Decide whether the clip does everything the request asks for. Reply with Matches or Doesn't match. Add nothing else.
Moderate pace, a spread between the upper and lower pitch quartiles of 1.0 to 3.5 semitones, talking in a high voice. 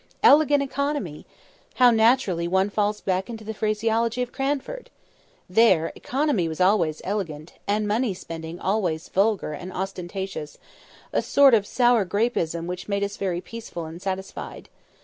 Doesn't match